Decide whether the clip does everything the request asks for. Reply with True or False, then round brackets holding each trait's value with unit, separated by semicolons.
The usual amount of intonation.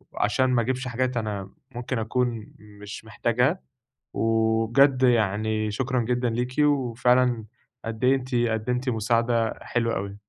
False (2.3 semitones)